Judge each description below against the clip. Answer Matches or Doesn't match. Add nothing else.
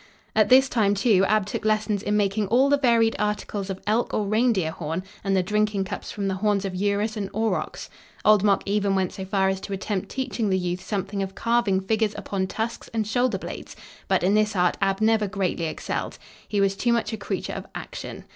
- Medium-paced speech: Doesn't match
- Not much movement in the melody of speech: Matches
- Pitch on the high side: Matches